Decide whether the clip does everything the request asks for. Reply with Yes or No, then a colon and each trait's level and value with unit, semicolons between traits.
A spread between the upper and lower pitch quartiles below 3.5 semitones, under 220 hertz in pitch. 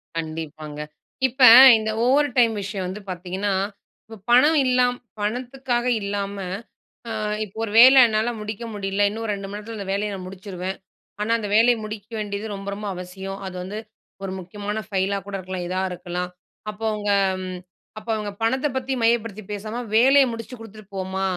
Yes: average, 3.1 semitones; high, 205 Hz